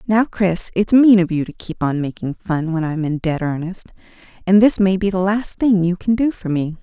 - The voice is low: No, medium, 185 Hz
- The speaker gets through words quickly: Yes, fast, 245 wpm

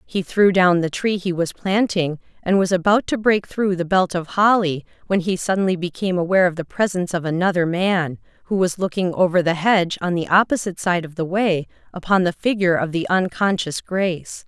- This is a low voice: No, medium, 180 Hz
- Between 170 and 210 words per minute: Yes, fast, 205 wpm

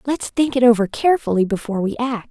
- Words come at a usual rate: No, fast, 210 wpm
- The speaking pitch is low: No, high, 235 Hz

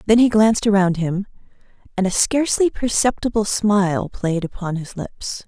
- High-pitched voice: Yes, high, 205 Hz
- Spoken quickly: No, average, 155 wpm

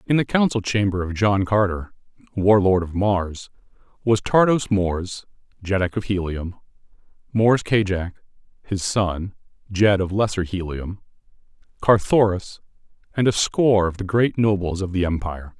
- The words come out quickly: No, slow, 135 wpm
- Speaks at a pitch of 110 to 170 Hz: No, low, 100 Hz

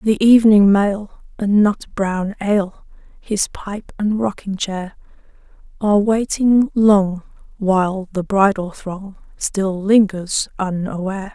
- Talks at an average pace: No, slow, 115 wpm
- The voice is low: No, high, 200 Hz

